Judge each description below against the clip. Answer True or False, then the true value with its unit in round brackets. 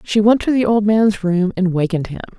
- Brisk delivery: True (250 wpm)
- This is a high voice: True (200 Hz)